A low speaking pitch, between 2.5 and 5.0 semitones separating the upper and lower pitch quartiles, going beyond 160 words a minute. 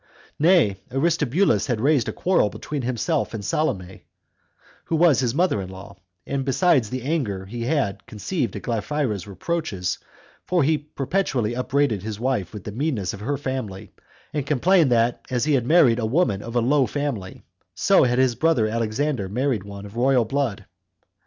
No: low, 125 Hz; wide, 5.6 semitones; average, 170 wpm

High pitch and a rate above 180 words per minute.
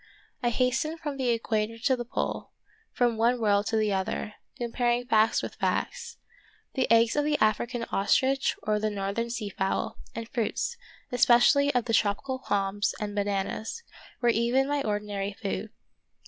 No: high, 230 Hz; average, 160 wpm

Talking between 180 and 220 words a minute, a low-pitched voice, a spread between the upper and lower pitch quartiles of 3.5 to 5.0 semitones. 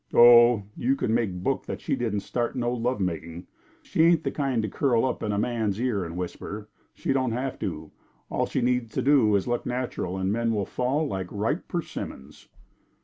Yes: average, 200 wpm; low, 115 Hz; average, 4.0 semitones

